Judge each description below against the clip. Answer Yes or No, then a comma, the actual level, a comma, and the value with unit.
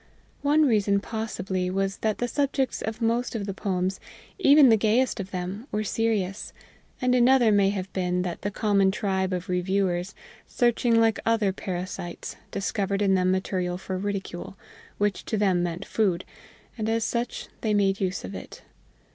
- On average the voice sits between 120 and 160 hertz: No, high, 200 Hz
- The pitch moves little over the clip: No, average, 3.2 semitones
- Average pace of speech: Yes, average, 165 wpm